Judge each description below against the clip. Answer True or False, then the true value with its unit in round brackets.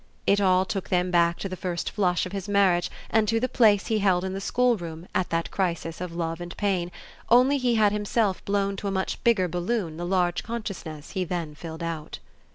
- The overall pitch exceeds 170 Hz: True (185 Hz)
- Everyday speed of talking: False (215 wpm)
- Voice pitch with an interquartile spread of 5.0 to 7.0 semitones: False (2.9 semitones)